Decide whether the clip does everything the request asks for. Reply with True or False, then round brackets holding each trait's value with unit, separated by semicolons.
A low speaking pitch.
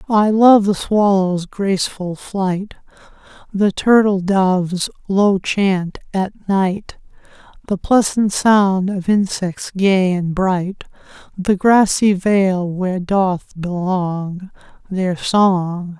False (190 Hz)